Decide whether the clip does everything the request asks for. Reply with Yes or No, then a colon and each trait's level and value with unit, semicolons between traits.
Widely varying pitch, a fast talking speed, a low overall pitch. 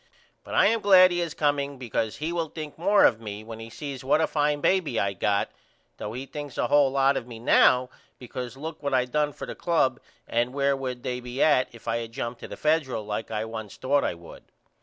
No: average, 4.3 semitones; fast, 240 wpm; low, 130 Hz